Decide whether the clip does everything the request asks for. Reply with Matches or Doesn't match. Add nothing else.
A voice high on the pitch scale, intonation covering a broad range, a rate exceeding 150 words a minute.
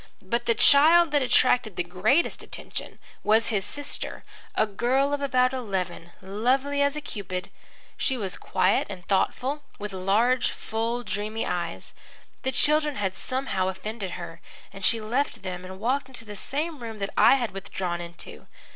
Matches